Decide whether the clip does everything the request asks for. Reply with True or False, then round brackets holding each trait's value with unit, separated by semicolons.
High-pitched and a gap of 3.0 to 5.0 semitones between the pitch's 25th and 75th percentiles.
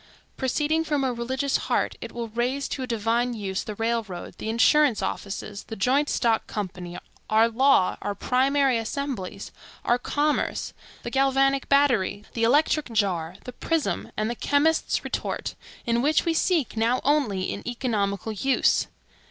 True (240 Hz; 4.3 semitones)